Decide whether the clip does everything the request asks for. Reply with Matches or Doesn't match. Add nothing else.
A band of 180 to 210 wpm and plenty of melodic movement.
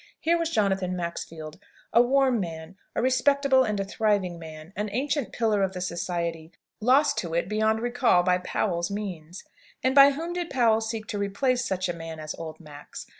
Matches